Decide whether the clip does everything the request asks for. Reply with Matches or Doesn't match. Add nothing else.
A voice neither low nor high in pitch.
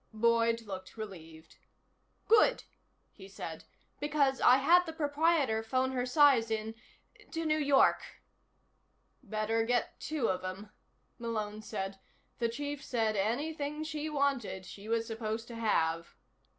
Doesn't match